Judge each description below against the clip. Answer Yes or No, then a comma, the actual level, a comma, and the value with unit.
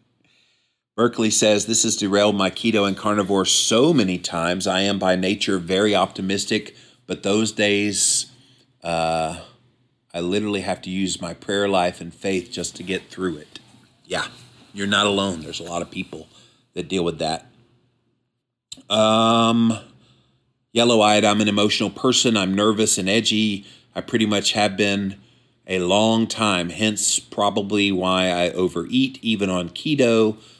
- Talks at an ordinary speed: Yes, average, 150 wpm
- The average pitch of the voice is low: Yes, low, 105 Hz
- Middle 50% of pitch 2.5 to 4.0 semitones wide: Yes, average, 3.2 semitones